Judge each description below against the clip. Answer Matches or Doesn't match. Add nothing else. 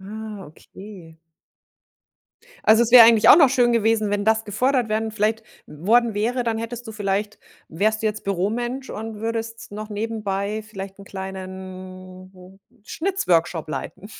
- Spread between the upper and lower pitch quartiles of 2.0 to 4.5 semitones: Matches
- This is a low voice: Doesn't match